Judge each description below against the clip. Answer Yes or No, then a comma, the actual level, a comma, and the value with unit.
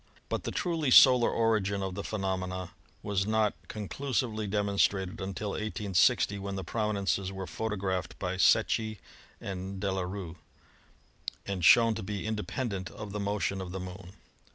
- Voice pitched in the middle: No, low, 100 Hz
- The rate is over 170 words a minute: No, average, 155 wpm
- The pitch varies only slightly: Yes, narrow, 2.3 semitones